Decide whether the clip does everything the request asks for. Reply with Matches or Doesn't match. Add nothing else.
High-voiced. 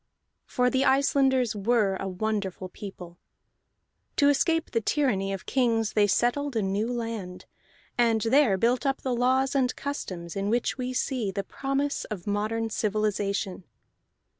Matches